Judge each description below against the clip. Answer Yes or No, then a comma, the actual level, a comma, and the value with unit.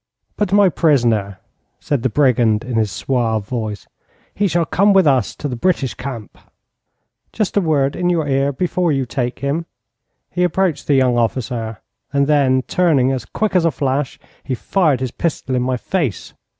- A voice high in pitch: No, low, 135 Hz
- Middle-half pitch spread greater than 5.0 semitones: Yes, wide, 5.4 semitones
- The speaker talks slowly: No, average, 175 wpm